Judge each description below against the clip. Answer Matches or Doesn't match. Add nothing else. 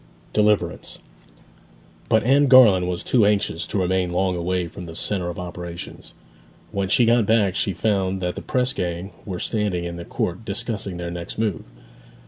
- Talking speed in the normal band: Matches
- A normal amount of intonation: Matches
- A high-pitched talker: Doesn't match